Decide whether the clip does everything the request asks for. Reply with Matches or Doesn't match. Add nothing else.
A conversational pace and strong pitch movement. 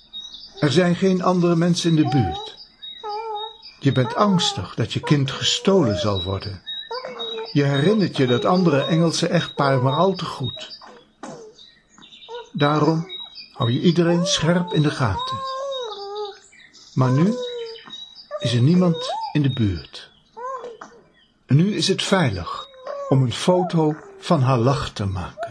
Doesn't match